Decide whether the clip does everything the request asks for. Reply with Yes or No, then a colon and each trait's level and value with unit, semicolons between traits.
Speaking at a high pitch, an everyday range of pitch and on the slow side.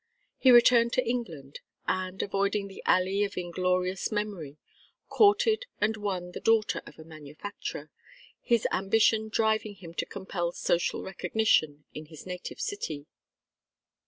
Yes: high, 195 Hz; average, 4.1 semitones; slow, 130 wpm